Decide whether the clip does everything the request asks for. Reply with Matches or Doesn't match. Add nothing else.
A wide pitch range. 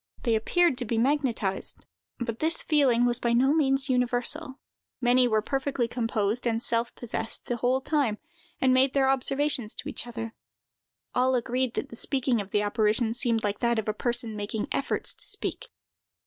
Doesn't match